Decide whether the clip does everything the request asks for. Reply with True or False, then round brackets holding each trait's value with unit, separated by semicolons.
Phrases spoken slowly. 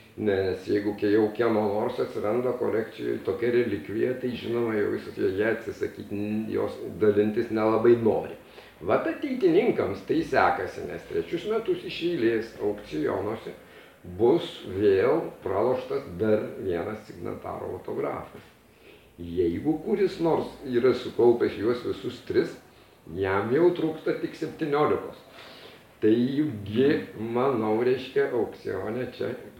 True (115 wpm)